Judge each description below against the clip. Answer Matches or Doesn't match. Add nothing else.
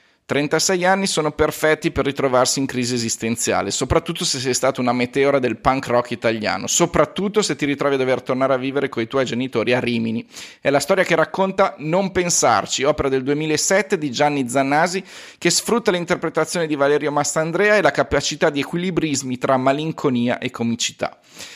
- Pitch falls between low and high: Matches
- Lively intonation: Doesn't match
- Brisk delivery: Matches